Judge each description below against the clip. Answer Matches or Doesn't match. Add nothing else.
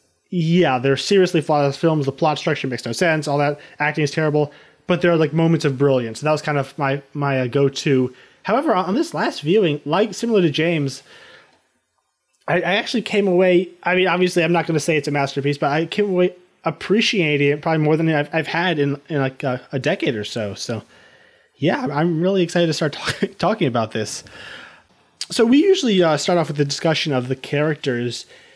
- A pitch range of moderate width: Matches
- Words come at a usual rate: Doesn't match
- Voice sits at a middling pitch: Matches